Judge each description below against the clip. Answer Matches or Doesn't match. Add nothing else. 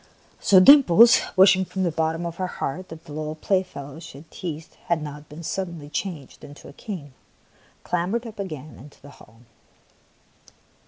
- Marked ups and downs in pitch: Doesn't match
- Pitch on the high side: Doesn't match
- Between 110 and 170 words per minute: Matches